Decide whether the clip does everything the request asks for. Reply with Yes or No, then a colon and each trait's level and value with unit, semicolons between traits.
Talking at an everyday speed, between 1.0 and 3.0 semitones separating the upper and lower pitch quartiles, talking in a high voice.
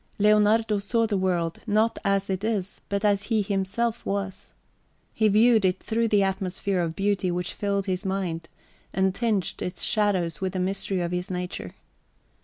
Yes: average, 170 wpm; narrow, 2.4 semitones; high, 195 Hz